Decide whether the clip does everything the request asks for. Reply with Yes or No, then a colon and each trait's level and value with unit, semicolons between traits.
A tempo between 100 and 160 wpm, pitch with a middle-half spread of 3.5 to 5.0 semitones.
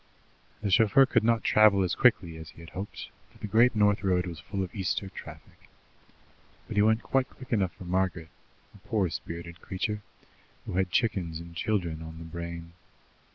No: average, 185 wpm; average, 3.8 semitones